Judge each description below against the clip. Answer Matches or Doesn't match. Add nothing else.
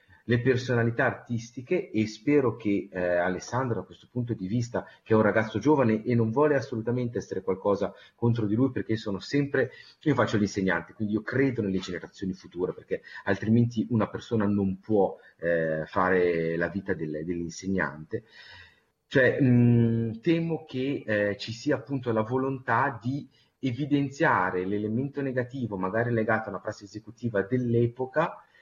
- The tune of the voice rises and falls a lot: Doesn't match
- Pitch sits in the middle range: Doesn't match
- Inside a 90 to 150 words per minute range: Matches